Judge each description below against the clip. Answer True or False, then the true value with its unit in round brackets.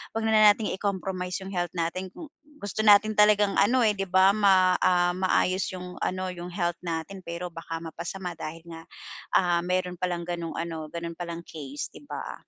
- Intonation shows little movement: True (2.3 semitones)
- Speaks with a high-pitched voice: False (180 Hz)